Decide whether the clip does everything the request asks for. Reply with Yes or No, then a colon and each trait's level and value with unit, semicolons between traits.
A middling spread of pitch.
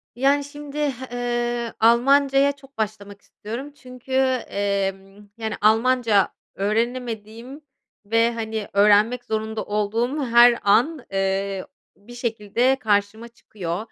Yes: average, 3.6 semitones